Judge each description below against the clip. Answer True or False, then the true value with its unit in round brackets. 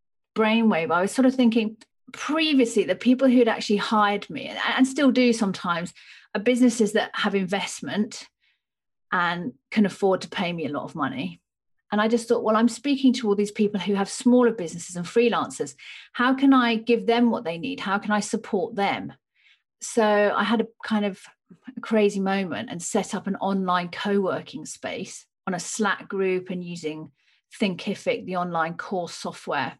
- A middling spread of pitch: True (3.6 semitones)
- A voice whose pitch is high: True (210 Hz)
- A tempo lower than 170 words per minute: False (175 wpm)